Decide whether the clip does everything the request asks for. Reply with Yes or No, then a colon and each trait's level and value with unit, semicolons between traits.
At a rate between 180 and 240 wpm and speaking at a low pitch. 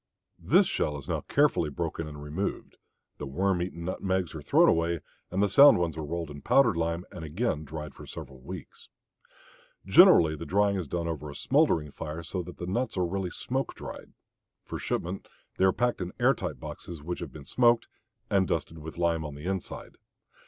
Yes: average, 195 wpm; very low, 85 Hz